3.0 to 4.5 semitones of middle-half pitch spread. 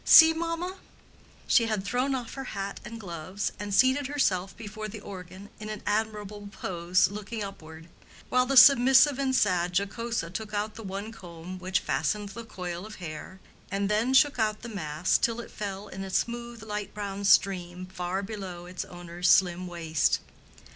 Yes: average, 3.9 semitones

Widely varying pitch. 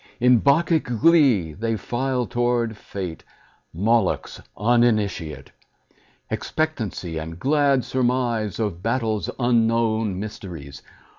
No: average, 3.9 semitones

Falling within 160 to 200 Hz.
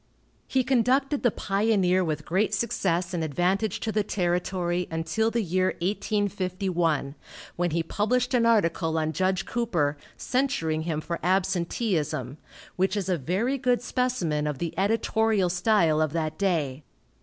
Yes: medium, 185 Hz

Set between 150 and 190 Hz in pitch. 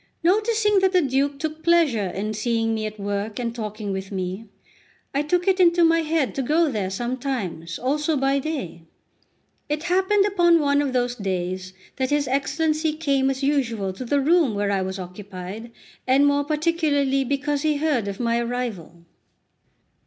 No: very high, 270 Hz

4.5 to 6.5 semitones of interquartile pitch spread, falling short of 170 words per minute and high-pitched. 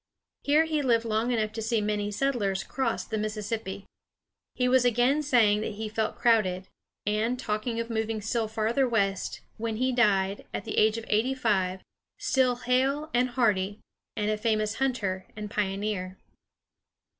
No: average, 2.8 semitones; average, 160 wpm; high, 220 Hz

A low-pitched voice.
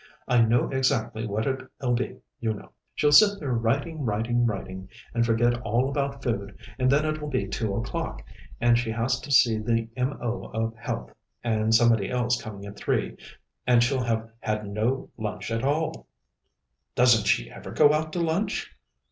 Yes: low, 120 Hz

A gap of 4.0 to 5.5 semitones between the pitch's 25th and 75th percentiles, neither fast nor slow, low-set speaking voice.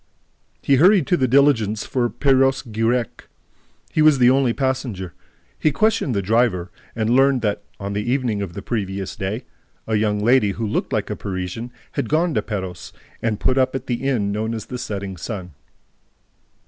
Yes: average, 4.6 semitones; average, 180 wpm; low, 115 Hz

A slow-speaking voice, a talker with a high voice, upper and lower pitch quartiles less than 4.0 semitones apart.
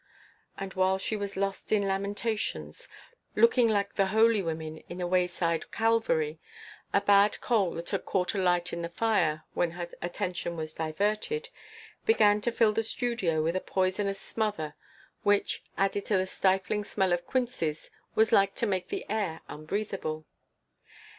No: average, 155 wpm; high, 195 Hz; average, 3.5 semitones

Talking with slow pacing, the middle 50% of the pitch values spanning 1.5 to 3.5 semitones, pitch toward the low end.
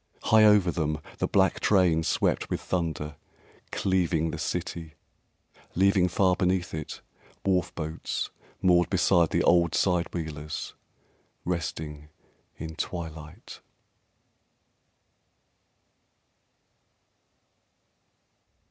Yes: slow, 85 wpm; narrow, 2.5 semitones; very low, 85 Hz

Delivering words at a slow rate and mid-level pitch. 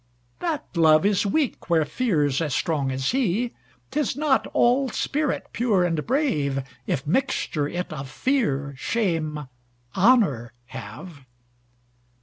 Yes: slow, 115 wpm; medium, 170 Hz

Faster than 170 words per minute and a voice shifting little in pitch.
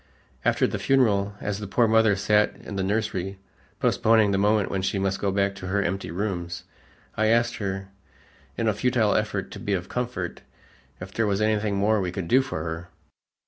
Yes: average, 195 wpm; narrow, 2.1 semitones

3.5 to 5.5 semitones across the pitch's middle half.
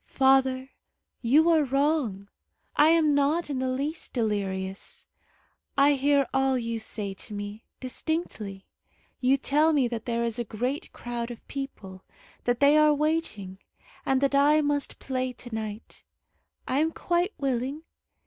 Yes: average, 4.0 semitones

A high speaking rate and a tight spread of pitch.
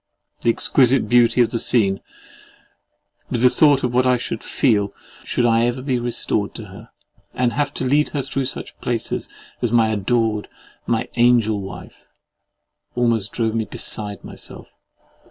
No: average, 155 wpm; narrow, 2.2 semitones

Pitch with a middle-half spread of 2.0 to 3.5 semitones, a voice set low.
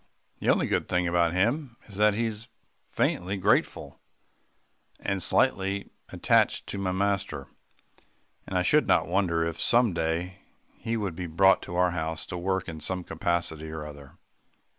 Yes: average, 3.1 semitones; very low, 90 Hz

